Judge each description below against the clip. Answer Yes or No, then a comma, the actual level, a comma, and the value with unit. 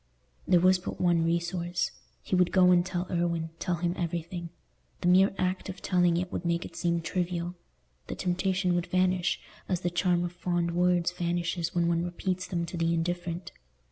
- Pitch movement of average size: No, narrow, 1.0 semitones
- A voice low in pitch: No, medium, 175 Hz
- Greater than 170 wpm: Yes, average, 180 wpm